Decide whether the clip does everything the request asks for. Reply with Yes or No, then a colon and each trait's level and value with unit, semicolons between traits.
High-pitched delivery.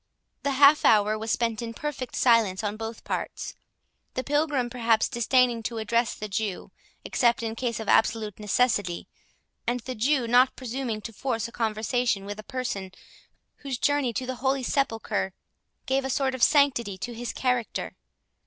Yes: high, 235 Hz